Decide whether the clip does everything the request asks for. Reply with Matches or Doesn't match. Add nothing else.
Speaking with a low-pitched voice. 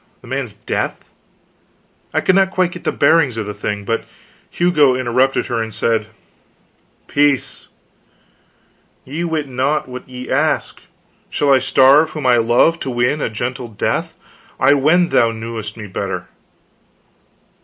Matches